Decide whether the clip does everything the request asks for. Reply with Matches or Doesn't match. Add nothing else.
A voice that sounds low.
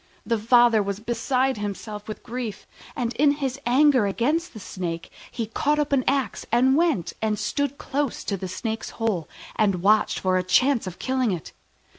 Doesn't match